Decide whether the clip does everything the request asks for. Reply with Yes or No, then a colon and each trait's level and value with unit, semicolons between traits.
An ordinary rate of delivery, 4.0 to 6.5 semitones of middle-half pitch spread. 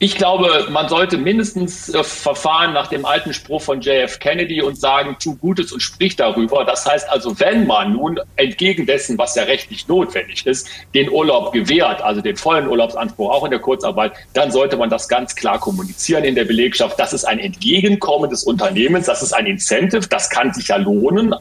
No: fast, 195 wpm; average, 4.7 semitones